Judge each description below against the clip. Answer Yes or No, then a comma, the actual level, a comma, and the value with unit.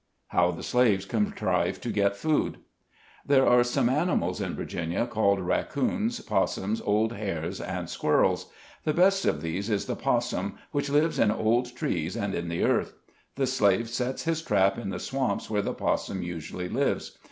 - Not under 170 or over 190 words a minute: Yes, average, 175 wpm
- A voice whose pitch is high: No, low, 110 Hz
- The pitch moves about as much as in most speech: No, wide, 5.7 semitones